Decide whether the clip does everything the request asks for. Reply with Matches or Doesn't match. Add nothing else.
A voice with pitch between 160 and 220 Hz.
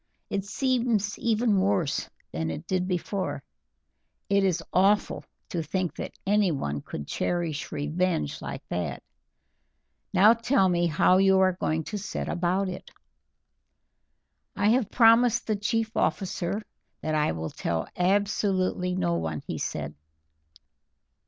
Matches